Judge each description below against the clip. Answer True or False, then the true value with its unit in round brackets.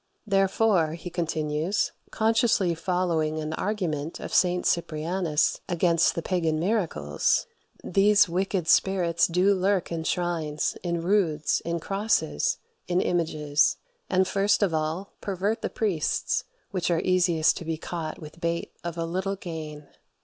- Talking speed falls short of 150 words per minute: True (135 wpm)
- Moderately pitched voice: True (175 Hz)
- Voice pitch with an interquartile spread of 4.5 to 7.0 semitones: False (3.2 semitones)